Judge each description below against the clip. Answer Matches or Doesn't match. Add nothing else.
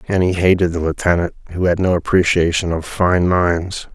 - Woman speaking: Doesn't match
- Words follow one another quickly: Doesn't match